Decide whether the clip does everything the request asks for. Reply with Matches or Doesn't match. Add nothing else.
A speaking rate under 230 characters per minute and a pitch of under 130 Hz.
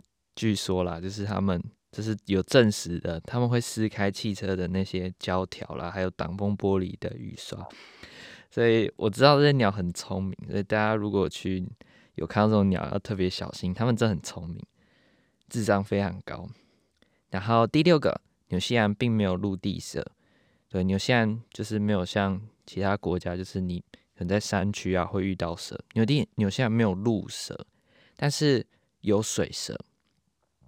Doesn't match